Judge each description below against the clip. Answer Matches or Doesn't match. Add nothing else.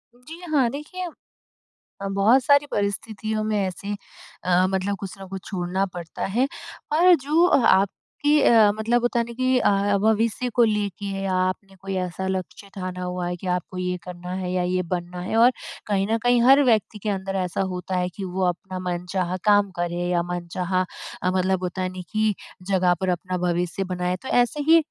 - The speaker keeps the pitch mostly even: Doesn't match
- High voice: Matches